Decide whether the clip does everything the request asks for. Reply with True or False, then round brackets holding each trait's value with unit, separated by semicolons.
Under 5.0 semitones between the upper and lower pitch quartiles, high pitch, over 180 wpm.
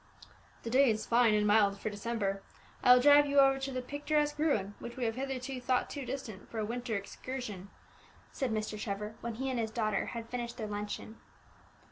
True (3.8 semitones; 235 Hz; 200 wpm)